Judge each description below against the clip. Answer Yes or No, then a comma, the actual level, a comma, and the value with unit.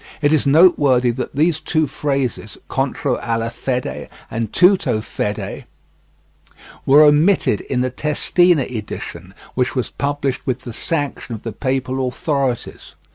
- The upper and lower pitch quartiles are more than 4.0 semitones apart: No, average, 3.6 semitones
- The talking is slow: Yes, slow, 130 wpm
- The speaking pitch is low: Yes, low, 130 Hz